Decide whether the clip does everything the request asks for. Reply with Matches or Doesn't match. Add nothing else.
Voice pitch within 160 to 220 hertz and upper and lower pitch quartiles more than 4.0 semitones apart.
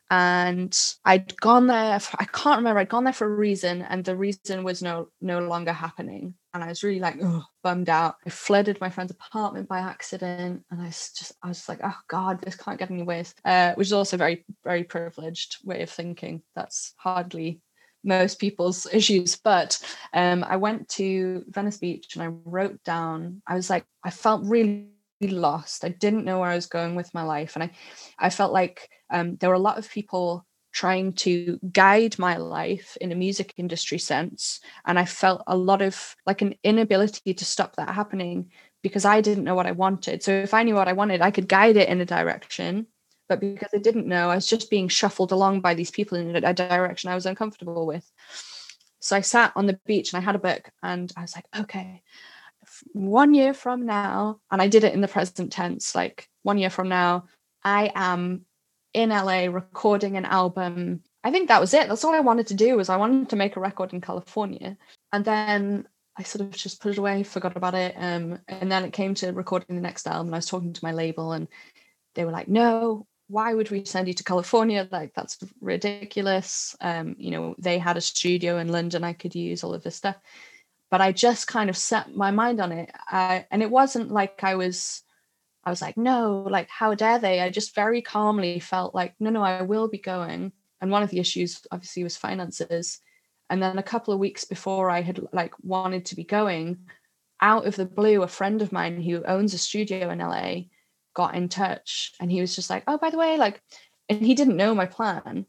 Doesn't match